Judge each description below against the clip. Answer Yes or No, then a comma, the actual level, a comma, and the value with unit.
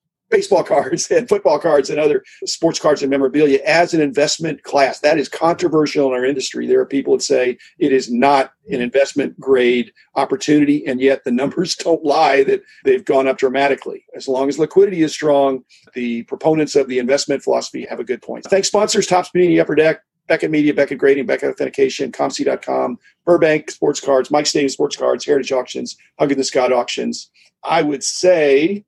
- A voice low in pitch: No, medium, 150 Hz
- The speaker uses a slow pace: No, average, 185 wpm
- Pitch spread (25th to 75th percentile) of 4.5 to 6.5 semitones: Yes, average, 5.0 semitones